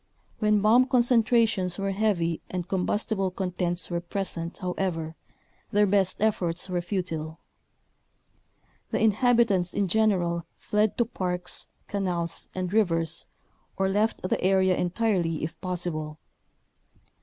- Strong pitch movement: No, average, 3.3 semitones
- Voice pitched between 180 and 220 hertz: Yes, medium, 185 Hz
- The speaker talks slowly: Yes, slow, 120 wpm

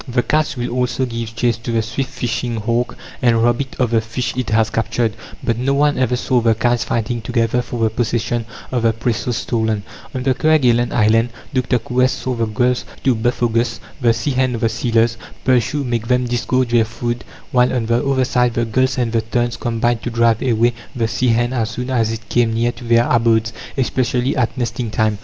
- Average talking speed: No, fast, 215 wpm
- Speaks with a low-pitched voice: Yes, low, 120 Hz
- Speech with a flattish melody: Yes, narrow, 1.6 semitones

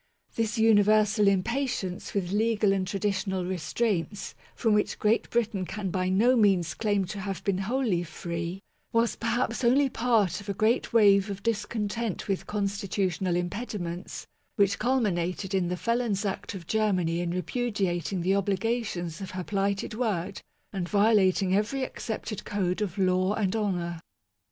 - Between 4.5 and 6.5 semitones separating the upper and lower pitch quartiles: No, average, 3.1 semitones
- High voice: Yes, high, 200 Hz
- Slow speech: No, average, 150 wpm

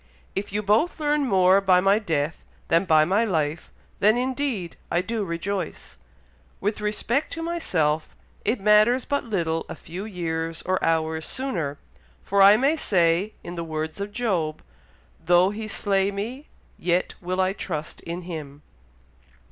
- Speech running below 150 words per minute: No, average, 155 wpm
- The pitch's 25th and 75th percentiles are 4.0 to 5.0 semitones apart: Yes, average, 4.5 semitones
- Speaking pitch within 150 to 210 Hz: Yes, high, 190 Hz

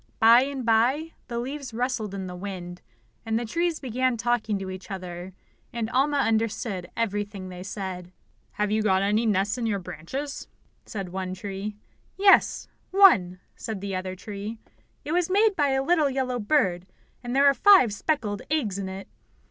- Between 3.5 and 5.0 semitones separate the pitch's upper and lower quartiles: No, wide, 5.6 semitones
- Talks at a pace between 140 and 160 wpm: No, average, 170 wpm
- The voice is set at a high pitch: Yes, high, 220 Hz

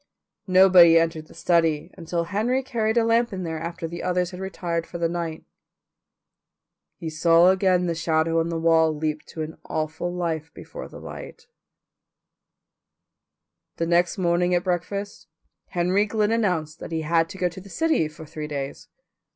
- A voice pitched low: No, medium, 170 Hz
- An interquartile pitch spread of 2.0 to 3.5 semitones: Yes, narrow, 2.4 semitones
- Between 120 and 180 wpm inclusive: Yes, average, 165 wpm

